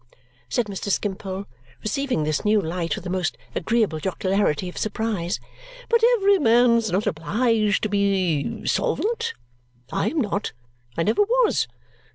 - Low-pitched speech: No, high, 205 Hz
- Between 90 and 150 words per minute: Yes, average, 140 wpm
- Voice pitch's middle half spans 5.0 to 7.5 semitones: No, average, 4.2 semitones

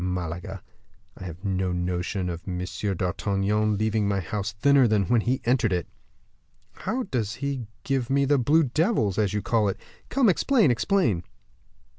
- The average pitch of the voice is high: No, low, 105 Hz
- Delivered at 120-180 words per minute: Yes, average, 160 wpm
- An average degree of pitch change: No, wide, 6.1 semitones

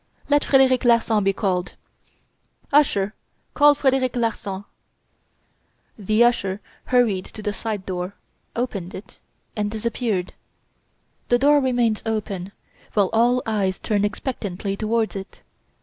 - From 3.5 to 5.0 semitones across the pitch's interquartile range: Yes, average, 3.8 semitones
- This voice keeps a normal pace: No, slow, 120 wpm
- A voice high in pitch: Yes, high, 215 Hz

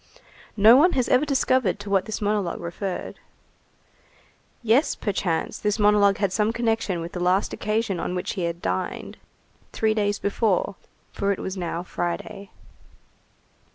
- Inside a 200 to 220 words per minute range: No, average, 150 wpm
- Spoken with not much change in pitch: No, average, 3.3 semitones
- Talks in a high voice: Yes, high, 200 Hz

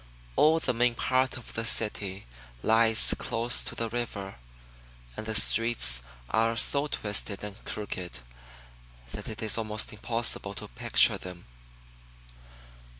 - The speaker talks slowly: Yes, slow, 130 wpm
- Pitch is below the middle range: Yes, low, 110 Hz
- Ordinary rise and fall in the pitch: No, narrow, 2.3 semitones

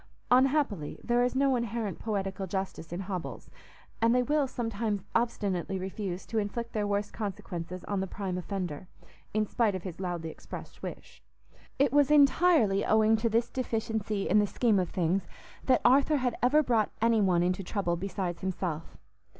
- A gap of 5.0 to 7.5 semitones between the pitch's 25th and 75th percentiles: No, average, 4.2 semitones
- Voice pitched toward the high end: Yes, high, 205 Hz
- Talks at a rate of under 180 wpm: Yes, average, 165 wpm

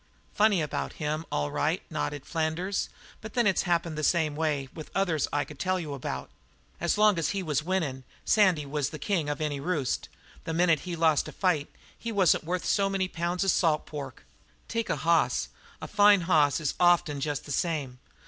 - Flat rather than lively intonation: No, average, 3.9 semitones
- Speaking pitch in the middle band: Yes, medium, 165 Hz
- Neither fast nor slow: Yes, average, 195 wpm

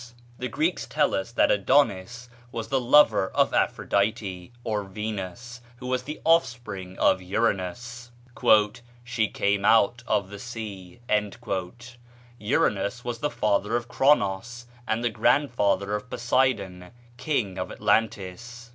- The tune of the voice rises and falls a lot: No, average, 3.7 semitones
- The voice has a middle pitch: No, low, 115 Hz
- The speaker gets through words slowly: Yes, slow, 125 wpm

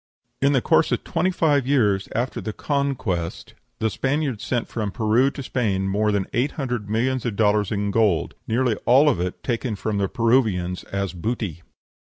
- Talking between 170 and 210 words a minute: Yes, average, 180 wpm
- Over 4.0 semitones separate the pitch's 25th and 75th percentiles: Yes, average, 4.6 semitones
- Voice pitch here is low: Yes, low, 110 Hz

